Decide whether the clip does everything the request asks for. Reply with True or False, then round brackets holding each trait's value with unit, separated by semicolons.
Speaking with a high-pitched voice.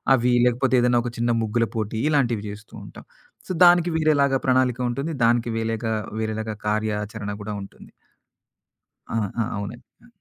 False (115 Hz)